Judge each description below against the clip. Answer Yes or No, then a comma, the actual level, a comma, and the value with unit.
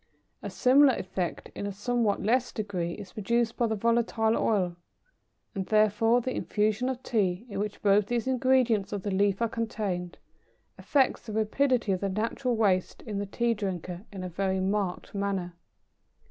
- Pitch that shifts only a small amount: No, average, 3.3 semitones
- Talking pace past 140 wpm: Yes, average, 170 wpm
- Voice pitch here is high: Yes, high, 210 Hz